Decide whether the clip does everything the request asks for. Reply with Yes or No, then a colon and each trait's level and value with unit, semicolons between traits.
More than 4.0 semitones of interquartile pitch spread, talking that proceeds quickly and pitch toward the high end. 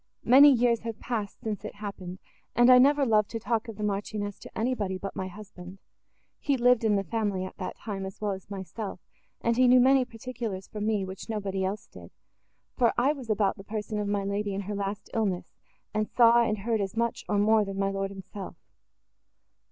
No: average, 2.9 semitones; fast, 210 wpm; high, 210 Hz